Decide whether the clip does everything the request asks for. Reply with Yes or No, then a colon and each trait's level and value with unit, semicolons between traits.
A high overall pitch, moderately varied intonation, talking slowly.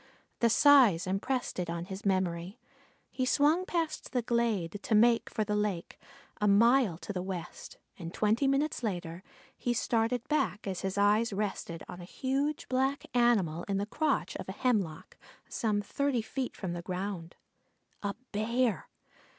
No: high, 210 Hz; average, 5.0 semitones; average, 160 wpm